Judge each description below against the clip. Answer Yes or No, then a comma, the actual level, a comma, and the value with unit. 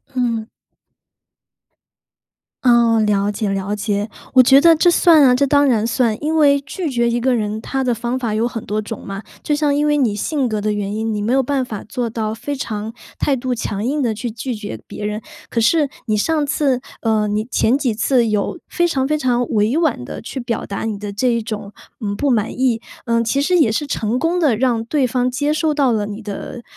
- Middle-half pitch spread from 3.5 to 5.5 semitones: Yes, average, 4.3 semitones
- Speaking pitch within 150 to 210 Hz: No, high, 235 Hz